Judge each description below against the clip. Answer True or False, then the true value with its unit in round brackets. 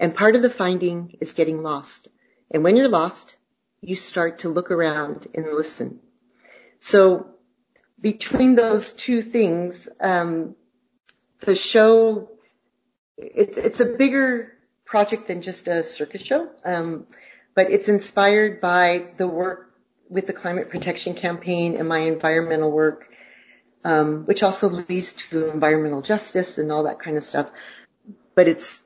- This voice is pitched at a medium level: True (180 Hz)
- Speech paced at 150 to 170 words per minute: False (140 wpm)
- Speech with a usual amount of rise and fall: True (4.5 semitones)